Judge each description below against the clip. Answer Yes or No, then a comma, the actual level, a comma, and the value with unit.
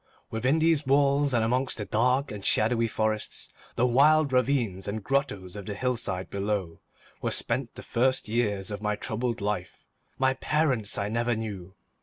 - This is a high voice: No, low, 115 Hz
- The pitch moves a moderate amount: Yes, average, 4.3 semitones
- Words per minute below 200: Yes, average, 165 wpm